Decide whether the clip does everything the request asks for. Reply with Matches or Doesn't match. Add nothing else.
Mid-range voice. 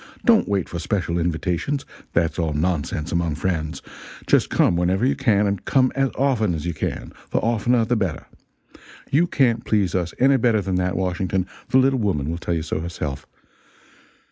Doesn't match